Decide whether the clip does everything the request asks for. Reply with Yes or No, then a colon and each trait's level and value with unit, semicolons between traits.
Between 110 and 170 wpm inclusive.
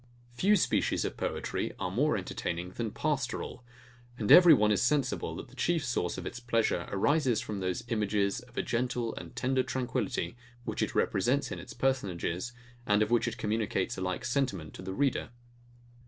No: average, 180 wpm